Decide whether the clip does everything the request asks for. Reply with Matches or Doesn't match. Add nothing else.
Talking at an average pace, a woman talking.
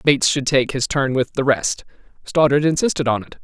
Doesn't match